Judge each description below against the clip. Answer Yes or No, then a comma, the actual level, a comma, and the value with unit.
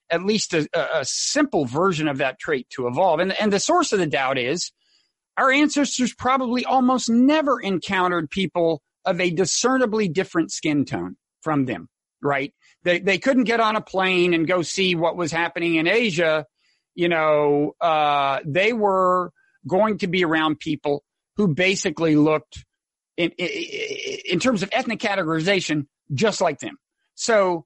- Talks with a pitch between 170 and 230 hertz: Yes, medium, 185 Hz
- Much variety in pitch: Yes, wide, 5.7 semitones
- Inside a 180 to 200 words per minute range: No, average, 160 wpm